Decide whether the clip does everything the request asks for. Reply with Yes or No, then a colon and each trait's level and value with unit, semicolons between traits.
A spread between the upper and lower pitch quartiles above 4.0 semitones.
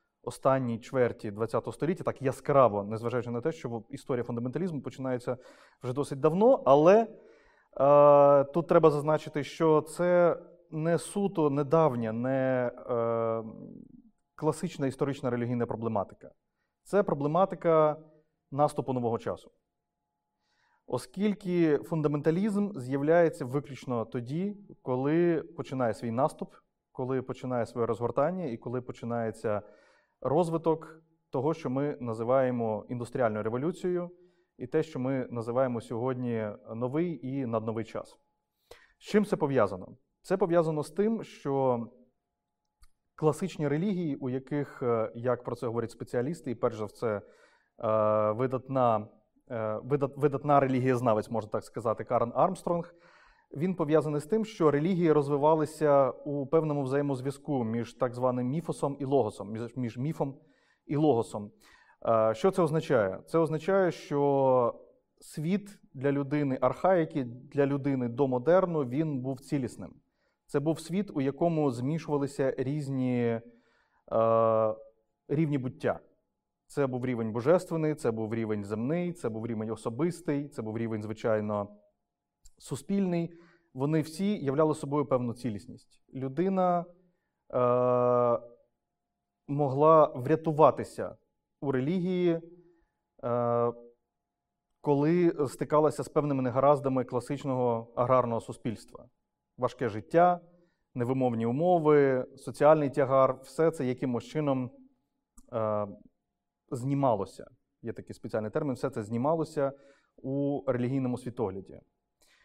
Yes: average, 4.7 semitones